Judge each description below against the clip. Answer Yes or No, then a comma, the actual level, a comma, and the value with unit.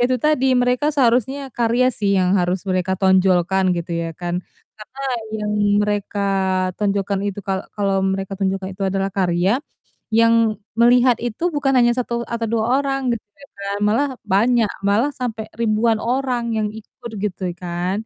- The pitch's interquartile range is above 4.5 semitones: No, average, 4.0 semitones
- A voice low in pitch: No, high, 210 Hz